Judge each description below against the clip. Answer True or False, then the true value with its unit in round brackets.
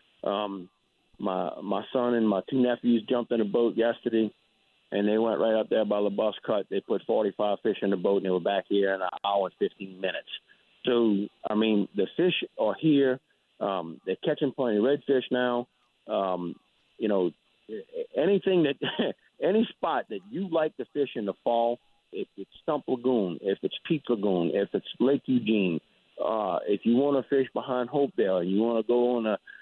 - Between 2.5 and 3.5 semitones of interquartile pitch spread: False (4.3 semitones)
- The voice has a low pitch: True (120 Hz)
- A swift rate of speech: False (195 wpm)